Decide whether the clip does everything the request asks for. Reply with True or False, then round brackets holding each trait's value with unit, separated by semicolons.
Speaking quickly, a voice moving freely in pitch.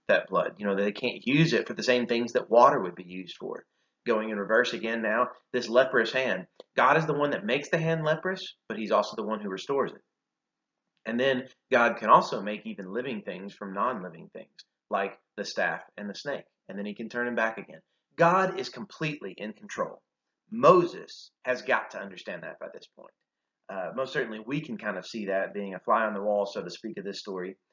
True (225 wpm; 7.3 semitones)